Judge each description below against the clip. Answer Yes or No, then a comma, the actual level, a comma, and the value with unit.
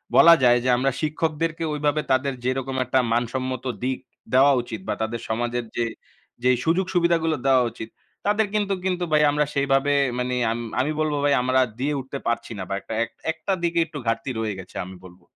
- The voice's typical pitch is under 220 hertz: Yes, low, 135 Hz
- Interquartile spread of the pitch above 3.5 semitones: Yes, average, 4.4 semitones